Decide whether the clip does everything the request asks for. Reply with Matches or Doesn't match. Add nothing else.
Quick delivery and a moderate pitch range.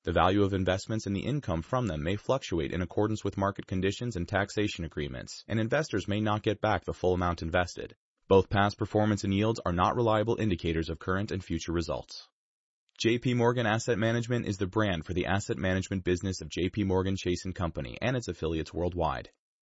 Doesn't match